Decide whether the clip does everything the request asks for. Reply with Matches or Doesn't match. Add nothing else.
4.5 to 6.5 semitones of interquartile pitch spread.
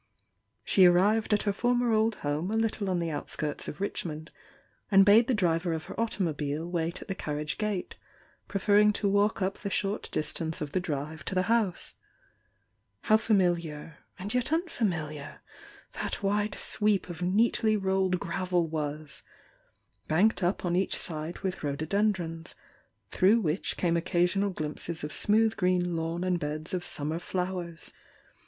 Doesn't match